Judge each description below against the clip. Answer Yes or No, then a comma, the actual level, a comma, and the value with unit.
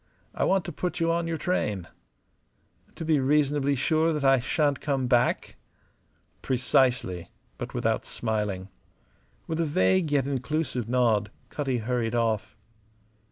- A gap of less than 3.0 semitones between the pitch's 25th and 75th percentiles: No, average, 4.8 semitones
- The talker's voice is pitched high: No, low, 135 Hz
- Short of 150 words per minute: Yes, slow, 135 wpm